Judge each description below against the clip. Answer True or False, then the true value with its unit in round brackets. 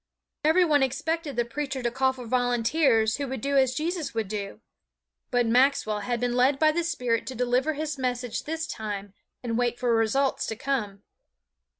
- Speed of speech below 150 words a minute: False (185 wpm)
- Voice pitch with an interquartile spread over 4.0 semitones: False (3.6 semitones)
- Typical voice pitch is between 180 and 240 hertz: False (250 Hz)